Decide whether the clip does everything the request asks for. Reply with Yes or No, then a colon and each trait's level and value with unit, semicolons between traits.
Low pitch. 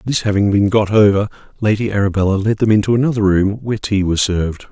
Yes: low, 105 Hz